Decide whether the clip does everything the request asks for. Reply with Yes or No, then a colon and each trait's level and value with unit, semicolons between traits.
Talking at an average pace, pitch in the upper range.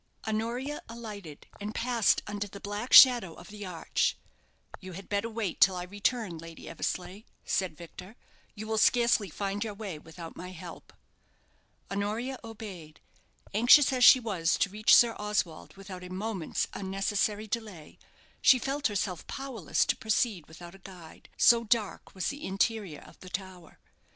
Yes: average, 155 wpm; high, 205 Hz